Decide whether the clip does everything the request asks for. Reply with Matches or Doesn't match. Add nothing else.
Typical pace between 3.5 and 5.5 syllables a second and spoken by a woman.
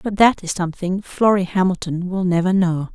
Matches